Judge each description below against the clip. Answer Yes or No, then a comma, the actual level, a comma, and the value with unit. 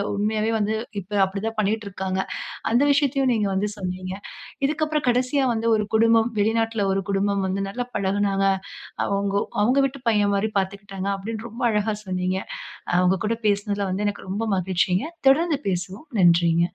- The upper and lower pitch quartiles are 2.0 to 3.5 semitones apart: Yes, average, 2.8 semitones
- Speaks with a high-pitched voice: Yes, high, 205 Hz